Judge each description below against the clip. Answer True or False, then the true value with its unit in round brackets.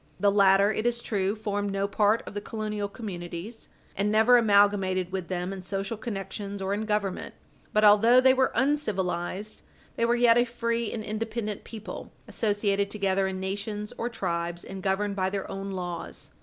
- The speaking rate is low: False (175 wpm)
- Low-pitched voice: False (205 Hz)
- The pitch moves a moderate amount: False (2.3 semitones)